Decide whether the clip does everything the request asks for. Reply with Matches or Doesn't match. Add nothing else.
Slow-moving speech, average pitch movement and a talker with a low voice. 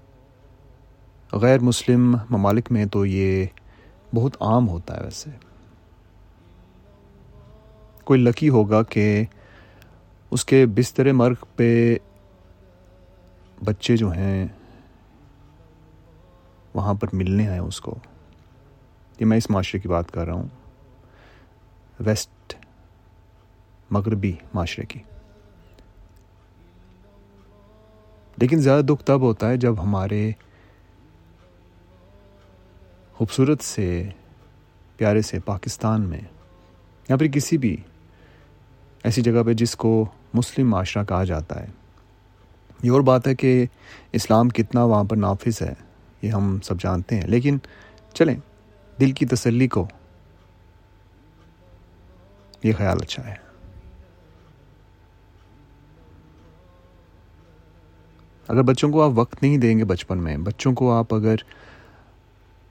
Matches